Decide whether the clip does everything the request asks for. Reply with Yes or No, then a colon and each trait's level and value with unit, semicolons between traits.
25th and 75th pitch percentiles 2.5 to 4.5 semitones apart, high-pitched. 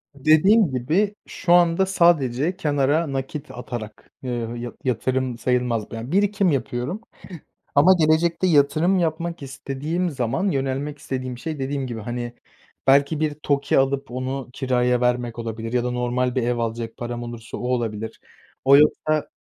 No: average, 4.2 semitones; low, 135 Hz